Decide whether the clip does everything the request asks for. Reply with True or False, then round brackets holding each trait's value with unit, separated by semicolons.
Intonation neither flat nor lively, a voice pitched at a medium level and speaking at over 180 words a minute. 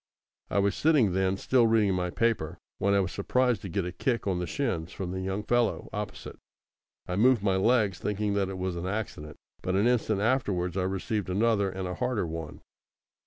False (3.4 semitones; 100 Hz; 205 wpm)